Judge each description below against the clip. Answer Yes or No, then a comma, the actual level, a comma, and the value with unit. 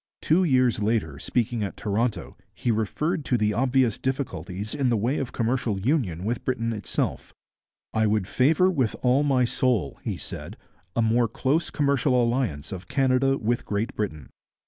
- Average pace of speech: Yes, average, 165 wpm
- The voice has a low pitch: Yes, low, 120 Hz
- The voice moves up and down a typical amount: Yes, average, 3.8 semitones